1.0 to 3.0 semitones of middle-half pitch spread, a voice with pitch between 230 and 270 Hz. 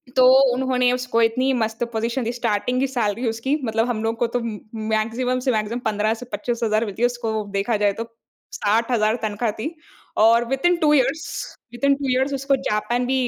Yes: narrow, 2.5 semitones; high, 235 Hz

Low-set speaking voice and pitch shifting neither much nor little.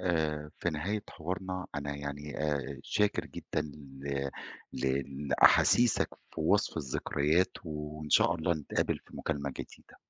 Yes: very low, 75 Hz; average, 3.3 semitones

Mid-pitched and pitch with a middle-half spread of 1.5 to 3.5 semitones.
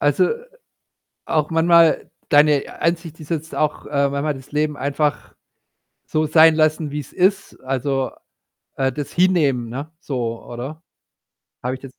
Yes: medium, 150 Hz; average, 2.8 semitones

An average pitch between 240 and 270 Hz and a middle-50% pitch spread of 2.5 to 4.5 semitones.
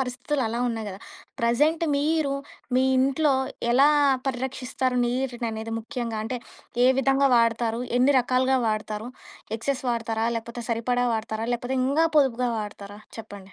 Yes: high, 245 Hz; average, 2.9 semitones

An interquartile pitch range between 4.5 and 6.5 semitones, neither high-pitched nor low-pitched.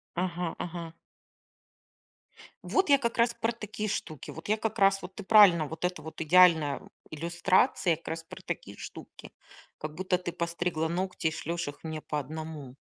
No: average, 3.5 semitones; medium, 175 Hz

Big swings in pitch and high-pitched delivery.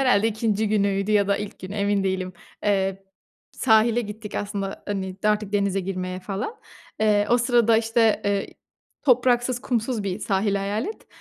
No: narrow, 2.4 semitones; high, 205 Hz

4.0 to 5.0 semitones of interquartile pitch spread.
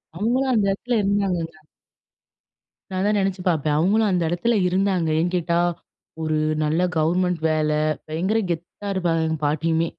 No: average, 3.6 semitones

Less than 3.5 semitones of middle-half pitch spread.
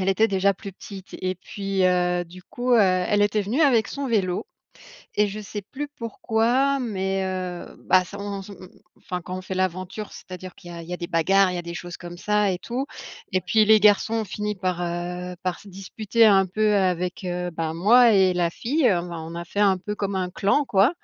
Yes: average, 2.7 semitones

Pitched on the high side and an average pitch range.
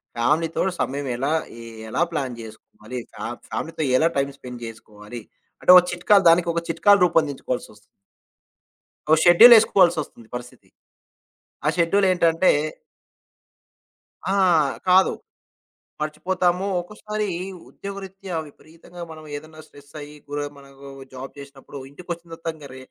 No: medium, 160 Hz; average, 4.5 semitones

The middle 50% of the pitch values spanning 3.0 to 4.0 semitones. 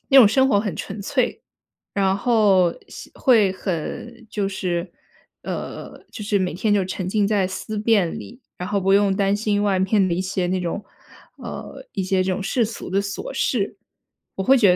No: narrow, 2.4 semitones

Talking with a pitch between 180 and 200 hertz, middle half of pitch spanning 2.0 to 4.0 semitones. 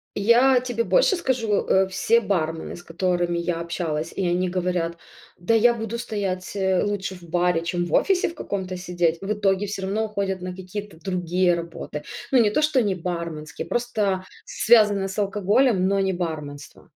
Yes: high, 190 Hz; average, 3.3 semitones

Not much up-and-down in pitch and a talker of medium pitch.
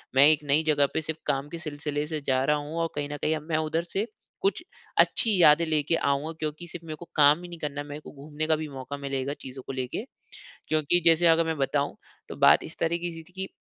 Yes: narrow, 2.3 semitones; medium, 155 Hz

